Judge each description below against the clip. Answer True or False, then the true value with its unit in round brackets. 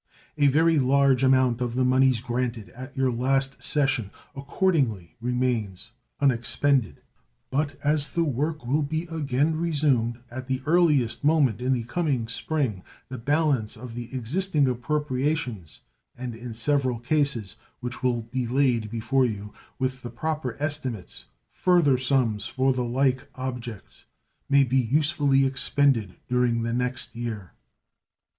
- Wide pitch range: False (3.2 semitones)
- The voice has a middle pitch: False (130 Hz)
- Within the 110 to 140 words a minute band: True (135 wpm)